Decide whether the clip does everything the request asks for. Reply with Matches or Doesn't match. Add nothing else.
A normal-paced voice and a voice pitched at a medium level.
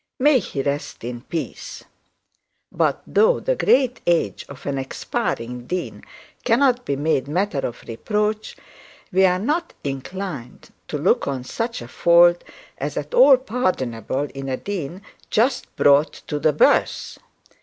Matches